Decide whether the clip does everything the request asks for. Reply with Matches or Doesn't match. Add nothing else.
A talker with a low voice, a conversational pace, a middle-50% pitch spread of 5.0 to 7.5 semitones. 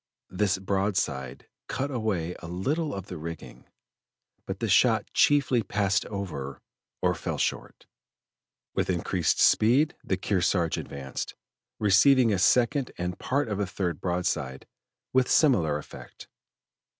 Doesn't match